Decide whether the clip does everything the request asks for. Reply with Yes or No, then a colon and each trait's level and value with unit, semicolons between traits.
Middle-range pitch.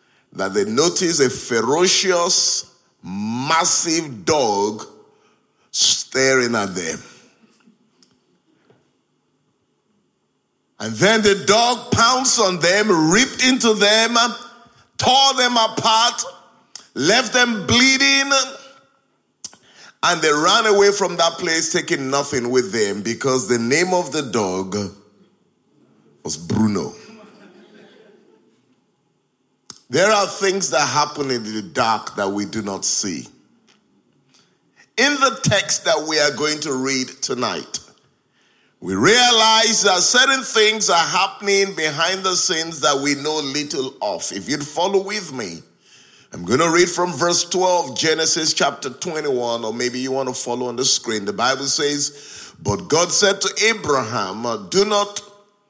Yes: medium, 175 Hz